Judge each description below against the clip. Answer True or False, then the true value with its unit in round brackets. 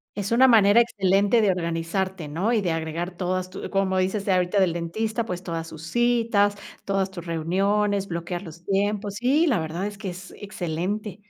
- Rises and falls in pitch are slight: False (3.2 semitones)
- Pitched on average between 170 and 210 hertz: True (190 Hz)